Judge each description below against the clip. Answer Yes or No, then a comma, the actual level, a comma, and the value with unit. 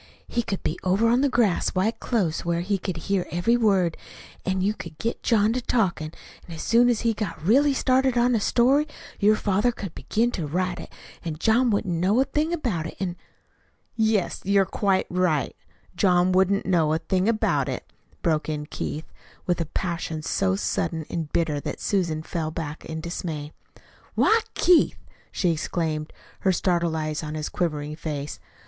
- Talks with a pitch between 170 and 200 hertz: Yes, medium, 185 Hz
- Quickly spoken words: No, average, 180 wpm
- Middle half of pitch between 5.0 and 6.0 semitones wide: Yes, average, 5.3 semitones